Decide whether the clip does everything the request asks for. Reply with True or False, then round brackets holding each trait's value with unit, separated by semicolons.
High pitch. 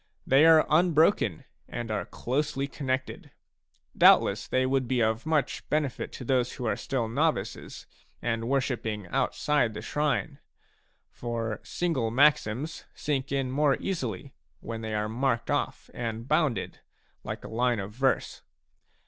False (130 Hz)